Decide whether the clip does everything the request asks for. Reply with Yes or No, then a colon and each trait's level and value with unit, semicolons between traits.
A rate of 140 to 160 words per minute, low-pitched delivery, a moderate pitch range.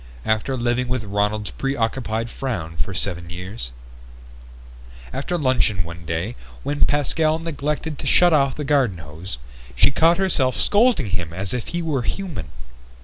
No: average, 145 wpm; low, 120 Hz; wide, 7.5 semitones